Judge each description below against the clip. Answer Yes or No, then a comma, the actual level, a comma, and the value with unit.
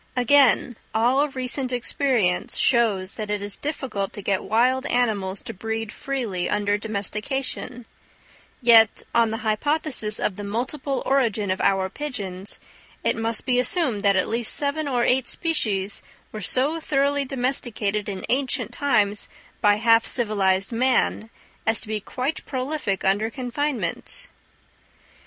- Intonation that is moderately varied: Yes, average, 4.3 semitones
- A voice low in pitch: No, high, 230 Hz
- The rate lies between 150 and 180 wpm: No, average, 140 wpm